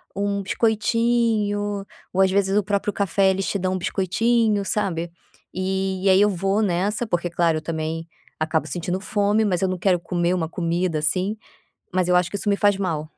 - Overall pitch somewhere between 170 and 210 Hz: Yes, high, 190 Hz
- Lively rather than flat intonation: No, average, 2.7 semitones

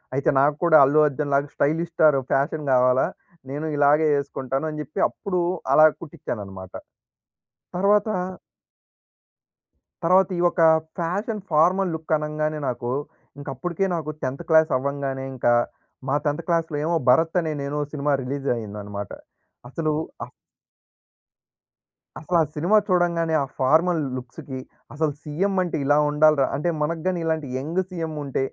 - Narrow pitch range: No, average, 3.3 semitones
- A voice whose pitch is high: No, medium, 155 Hz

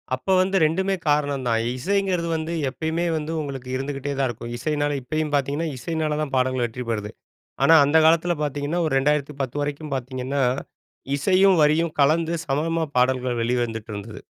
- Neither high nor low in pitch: Yes, medium, 145 Hz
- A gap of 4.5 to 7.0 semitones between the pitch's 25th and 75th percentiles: No, average, 3.7 semitones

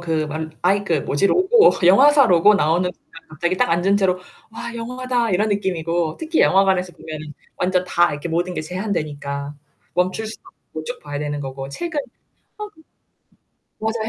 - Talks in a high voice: No, medium, 180 Hz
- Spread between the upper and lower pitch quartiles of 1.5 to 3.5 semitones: No, average, 5.3 semitones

